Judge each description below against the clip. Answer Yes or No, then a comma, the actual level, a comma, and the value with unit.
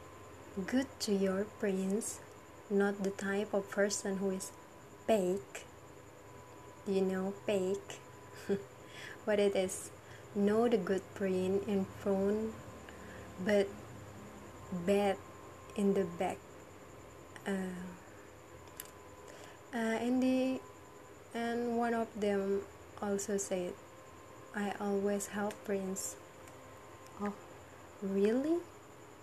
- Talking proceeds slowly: Yes, slow, 90 wpm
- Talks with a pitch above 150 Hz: Yes, high, 190 Hz